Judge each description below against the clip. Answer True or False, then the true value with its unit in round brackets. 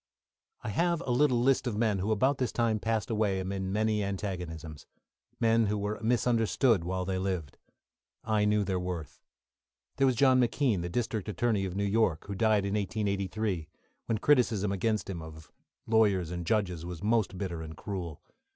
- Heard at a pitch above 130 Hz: False (105 Hz)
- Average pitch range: True (3.5 semitones)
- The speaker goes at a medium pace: True (175 wpm)